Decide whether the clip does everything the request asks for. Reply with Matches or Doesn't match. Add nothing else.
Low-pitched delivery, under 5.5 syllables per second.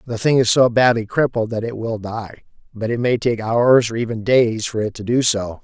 Matches